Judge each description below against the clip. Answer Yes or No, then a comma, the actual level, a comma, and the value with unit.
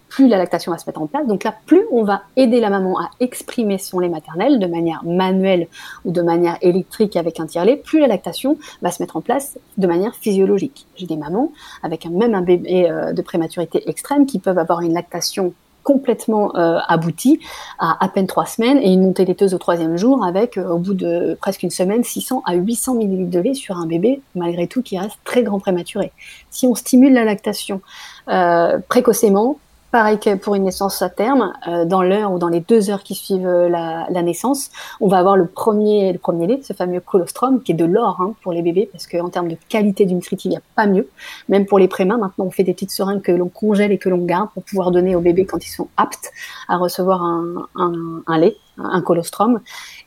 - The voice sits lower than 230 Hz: Yes, high, 190 Hz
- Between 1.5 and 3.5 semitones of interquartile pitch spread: No, average, 3.9 semitones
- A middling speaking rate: No, fast, 225 wpm